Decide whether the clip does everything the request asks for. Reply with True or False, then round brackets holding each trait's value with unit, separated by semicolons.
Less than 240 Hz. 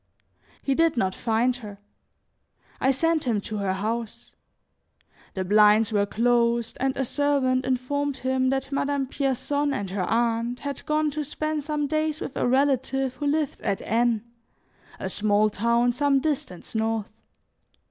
False (255 Hz)